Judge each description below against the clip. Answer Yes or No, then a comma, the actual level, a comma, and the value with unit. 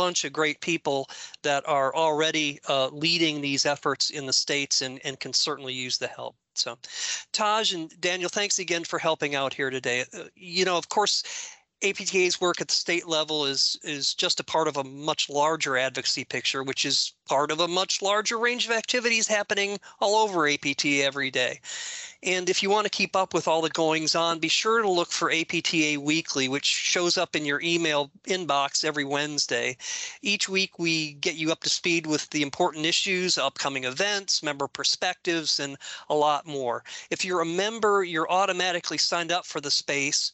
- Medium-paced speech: Yes, average, 190 wpm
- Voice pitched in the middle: Yes, medium, 160 Hz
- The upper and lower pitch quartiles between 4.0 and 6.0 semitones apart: Yes, average, 4.4 semitones